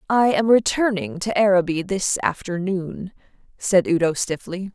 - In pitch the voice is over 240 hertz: No, high, 190 Hz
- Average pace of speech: No, slow, 125 wpm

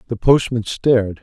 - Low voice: Yes, low, 115 Hz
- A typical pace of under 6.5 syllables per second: Yes, 4.9 syllables/s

